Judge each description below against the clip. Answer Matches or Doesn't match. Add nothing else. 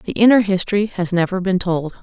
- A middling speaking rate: Doesn't match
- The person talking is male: Doesn't match